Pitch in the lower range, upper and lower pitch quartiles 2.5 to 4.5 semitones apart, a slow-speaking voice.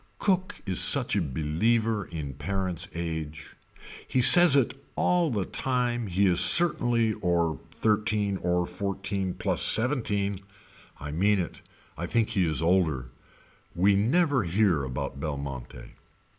No: very low, 95 Hz; wide, 5.5 semitones; slow, 130 wpm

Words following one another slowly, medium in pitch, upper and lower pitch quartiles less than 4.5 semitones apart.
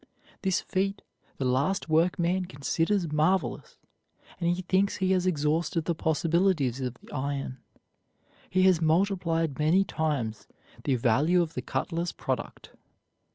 Yes: slow, 130 wpm; medium, 165 Hz; average, 3.8 semitones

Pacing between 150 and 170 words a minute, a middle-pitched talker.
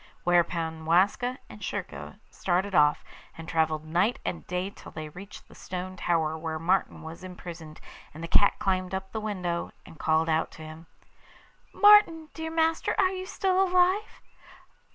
Yes: average, 160 wpm; medium, 180 Hz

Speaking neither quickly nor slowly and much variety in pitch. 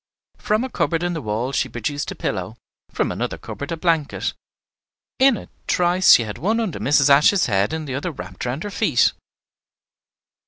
Yes: average, 185 wpm; wide, 6.4 semitones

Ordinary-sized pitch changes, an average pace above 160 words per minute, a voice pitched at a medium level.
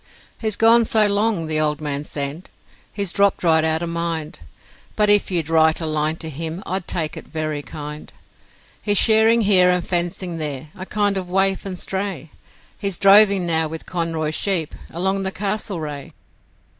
Yes: average, 3.9 semitones; average, 170 wpm; medium, 175 Hz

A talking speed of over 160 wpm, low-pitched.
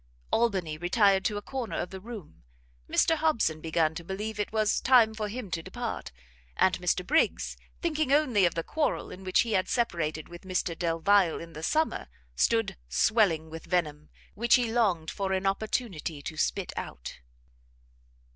No: average, 170 wpm; high, 190 Hz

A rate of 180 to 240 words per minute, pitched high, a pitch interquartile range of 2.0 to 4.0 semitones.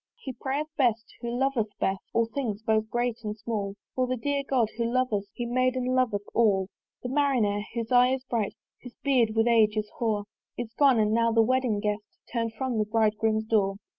Yes: fast, 205 wpm; high, 230 Hz; average, 2.9 semitones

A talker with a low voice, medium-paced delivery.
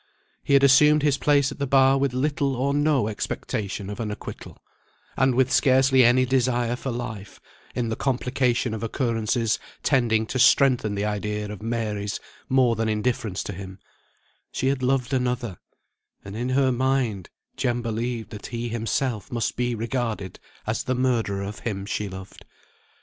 Yes: low, 120 Hz; average, 165 wpm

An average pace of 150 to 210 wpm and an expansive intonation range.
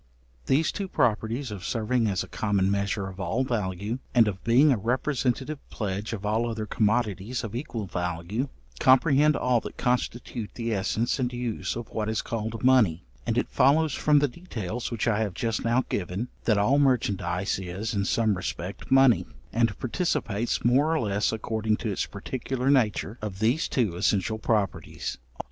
No: average, 170 wpm; average, 3.7 semitones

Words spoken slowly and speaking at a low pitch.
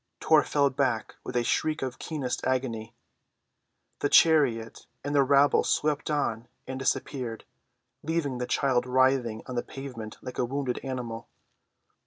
No: average, 145 wpm; low, 130 Hz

